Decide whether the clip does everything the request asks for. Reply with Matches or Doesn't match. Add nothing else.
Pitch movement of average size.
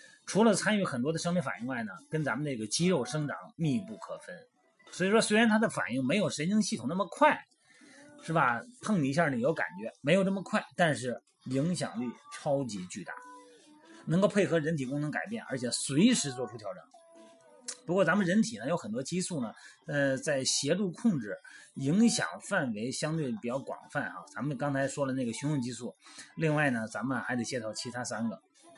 Doesn't match